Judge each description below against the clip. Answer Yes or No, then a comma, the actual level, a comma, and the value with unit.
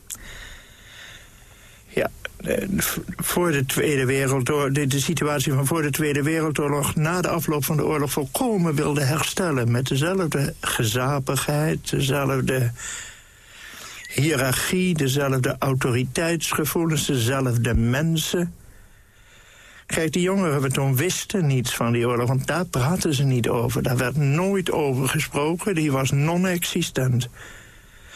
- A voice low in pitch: No, medium, 145 Hz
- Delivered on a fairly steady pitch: No, average, 3.3 semitones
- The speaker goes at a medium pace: No, slow, 115 wpm